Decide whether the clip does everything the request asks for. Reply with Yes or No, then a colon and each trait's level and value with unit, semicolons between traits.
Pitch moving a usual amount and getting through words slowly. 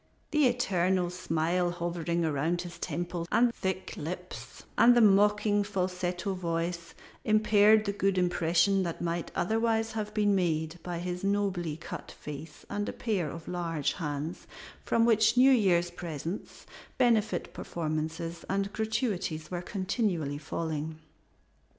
Yes: average, 3.7 semitones; slow, 130 wpm